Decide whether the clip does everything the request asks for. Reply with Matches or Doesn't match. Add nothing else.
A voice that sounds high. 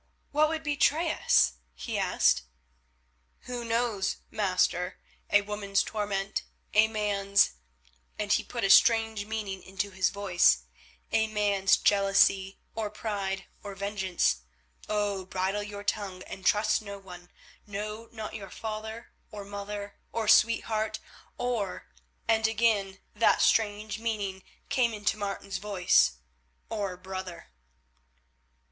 Matches